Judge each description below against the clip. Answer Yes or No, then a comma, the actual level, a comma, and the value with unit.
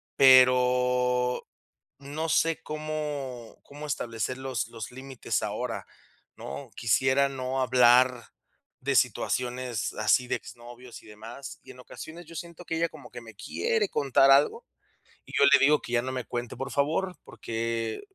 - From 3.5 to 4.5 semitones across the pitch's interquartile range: No, average, 2.9 semitones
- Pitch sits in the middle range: No, low, 130 Hz